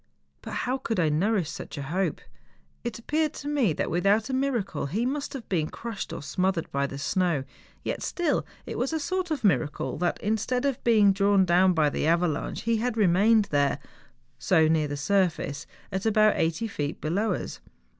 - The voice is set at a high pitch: Yes, high, 195 Hz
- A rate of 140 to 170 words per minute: No, average, 190 wpm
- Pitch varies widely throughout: Yes, wide, 6.3 semitones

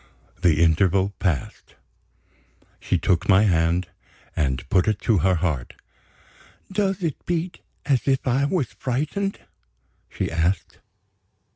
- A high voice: No, low, 100 Hz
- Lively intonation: Yes, wide, 8.7 semitones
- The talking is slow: Yes, slow, 120 wpm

